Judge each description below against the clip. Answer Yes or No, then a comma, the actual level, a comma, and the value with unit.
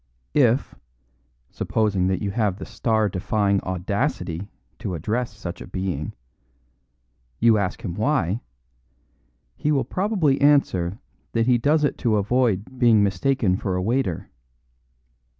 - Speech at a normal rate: No, slow, 130 wpm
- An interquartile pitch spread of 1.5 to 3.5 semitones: No, average, 5.1 semitones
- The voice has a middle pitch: No, low, 105 Hz